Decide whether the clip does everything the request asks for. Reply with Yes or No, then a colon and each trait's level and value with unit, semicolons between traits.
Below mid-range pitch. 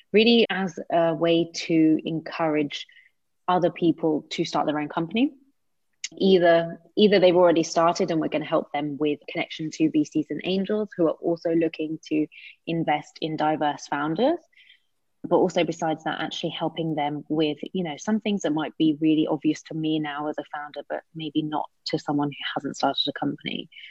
No: medium, 160 Hz